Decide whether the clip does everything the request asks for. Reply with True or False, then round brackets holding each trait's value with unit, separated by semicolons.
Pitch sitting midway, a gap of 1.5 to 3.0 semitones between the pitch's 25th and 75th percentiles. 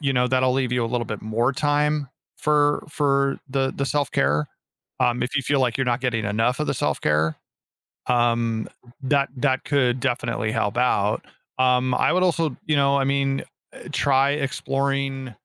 False (130 Hz; 2.6 semitones)